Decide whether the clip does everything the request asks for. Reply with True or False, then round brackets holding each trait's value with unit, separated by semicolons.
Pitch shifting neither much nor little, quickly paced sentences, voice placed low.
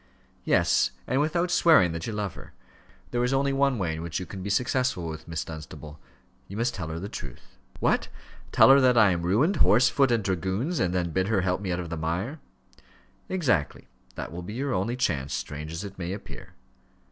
False (6.8 semitones; 215 wpm; 95 Hz)